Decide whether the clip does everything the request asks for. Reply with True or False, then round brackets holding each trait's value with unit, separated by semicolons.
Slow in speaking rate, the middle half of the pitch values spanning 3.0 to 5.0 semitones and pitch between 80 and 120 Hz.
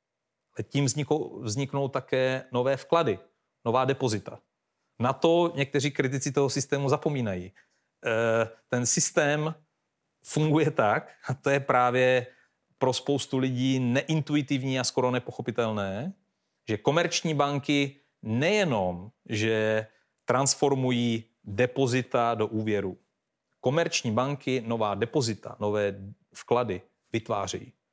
False (100 wpm; 3.8 semitones; 130 Hz)